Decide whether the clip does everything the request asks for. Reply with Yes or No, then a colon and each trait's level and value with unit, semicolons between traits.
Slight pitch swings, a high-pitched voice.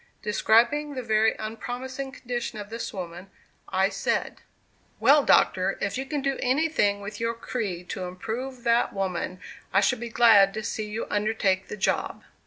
No: average, 3.9 semitones; high, 220 Hz